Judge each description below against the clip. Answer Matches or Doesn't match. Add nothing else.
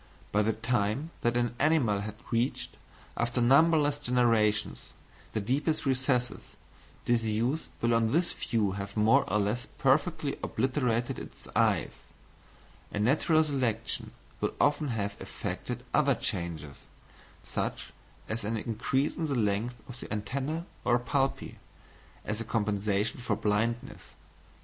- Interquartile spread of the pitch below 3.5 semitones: Doesn't match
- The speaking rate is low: Matches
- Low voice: Matches